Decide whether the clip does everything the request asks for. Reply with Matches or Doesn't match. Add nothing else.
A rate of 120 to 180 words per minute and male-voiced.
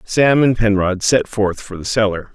Doesn't match